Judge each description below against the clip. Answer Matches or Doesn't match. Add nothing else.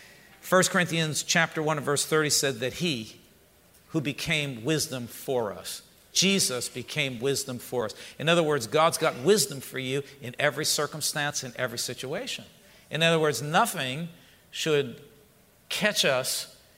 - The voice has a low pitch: Doesn't match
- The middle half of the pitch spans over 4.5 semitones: Doesn't match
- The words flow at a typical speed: Matches